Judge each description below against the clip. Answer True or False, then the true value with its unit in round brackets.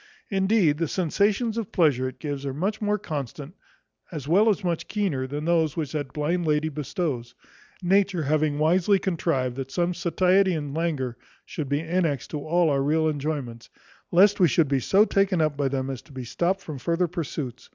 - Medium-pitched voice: True (155 Hz)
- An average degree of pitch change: True (4.4 semitones)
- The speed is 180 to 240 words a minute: True (190 wpm)